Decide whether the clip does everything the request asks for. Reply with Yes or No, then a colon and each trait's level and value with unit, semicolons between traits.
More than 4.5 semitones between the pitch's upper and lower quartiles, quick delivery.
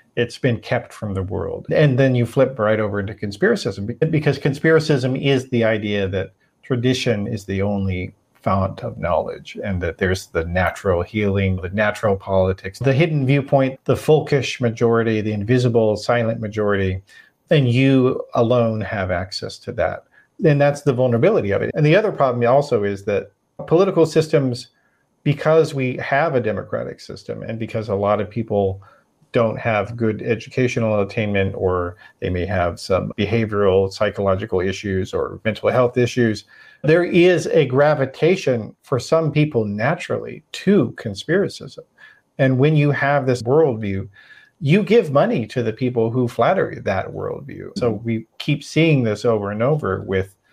No: average, 5.2 semitones; average, 160 wpm